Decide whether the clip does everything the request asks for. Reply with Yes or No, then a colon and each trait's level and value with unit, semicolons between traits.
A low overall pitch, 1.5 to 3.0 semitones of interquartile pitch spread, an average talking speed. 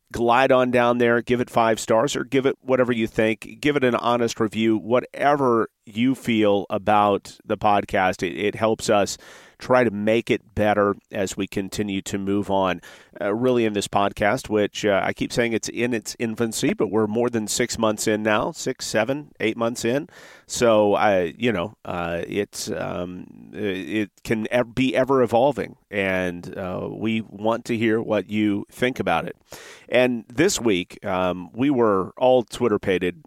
Yes: low, 110 Hz; average, 2.7 semitones; average, 175 wpm